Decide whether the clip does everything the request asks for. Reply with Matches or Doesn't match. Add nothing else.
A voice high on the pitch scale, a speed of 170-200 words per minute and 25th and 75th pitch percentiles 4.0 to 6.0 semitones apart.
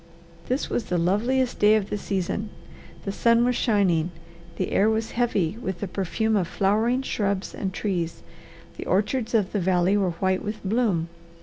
Doesn't match